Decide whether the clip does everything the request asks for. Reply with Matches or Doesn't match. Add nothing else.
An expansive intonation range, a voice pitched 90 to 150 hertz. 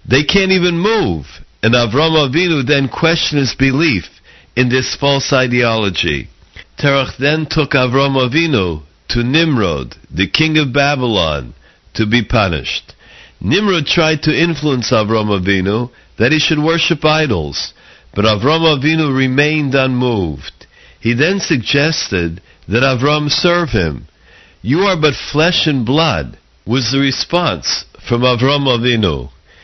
Matches